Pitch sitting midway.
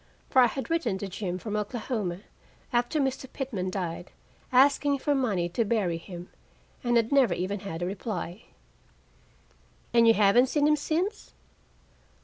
No: high, 225 Hz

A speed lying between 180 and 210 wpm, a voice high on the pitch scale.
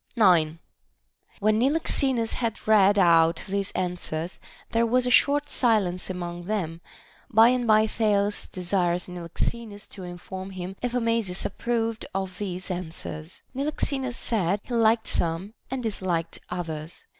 No: slow, 135 wpm; high, 200 Hz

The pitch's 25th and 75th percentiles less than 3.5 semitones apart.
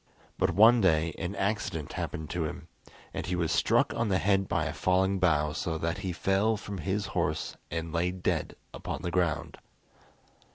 Yes: average, 3.1 semitones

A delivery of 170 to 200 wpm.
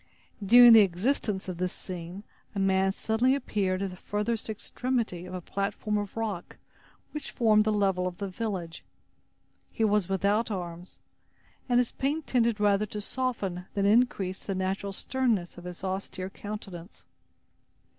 No: average, 155 wpm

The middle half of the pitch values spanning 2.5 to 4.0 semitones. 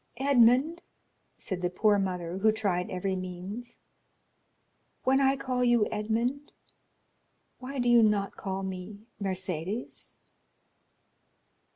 No: average, 4.6 semitones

